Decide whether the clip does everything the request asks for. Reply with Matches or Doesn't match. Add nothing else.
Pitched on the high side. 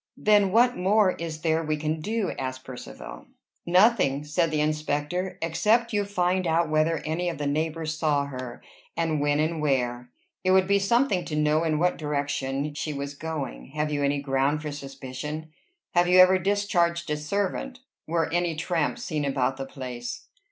Doesn't match